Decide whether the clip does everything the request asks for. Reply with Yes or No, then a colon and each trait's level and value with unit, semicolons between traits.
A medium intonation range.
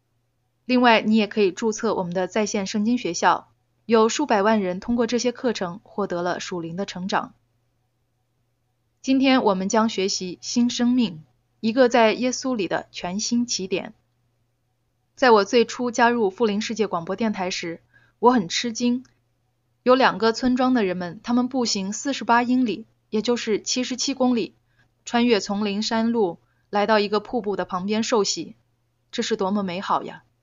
No: wide, 5.9 semitones